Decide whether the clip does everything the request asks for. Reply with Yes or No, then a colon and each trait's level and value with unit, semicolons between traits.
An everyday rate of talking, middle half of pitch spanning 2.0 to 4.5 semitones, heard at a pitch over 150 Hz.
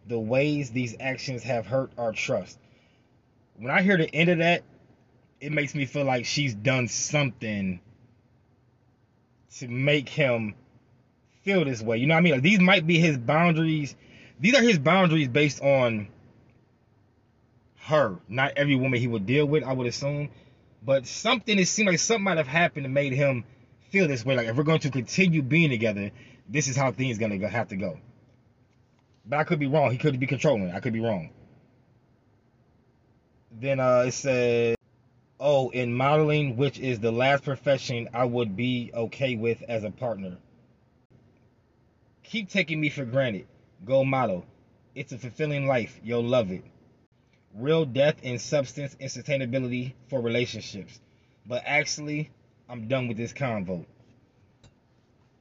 No: average, 165 wpm; average, 3.2 semitones; low, 125 Hz